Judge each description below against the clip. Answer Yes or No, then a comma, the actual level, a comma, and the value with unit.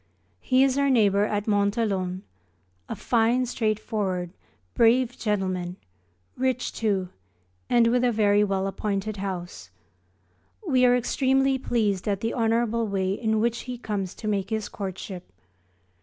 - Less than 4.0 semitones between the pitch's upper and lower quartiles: Yes, average, 3.5 semitones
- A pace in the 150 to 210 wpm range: No, slow, 135 wpm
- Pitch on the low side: No, high, 215 Hz